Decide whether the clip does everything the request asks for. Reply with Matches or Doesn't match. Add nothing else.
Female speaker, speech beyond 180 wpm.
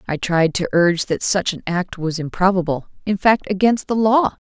Matches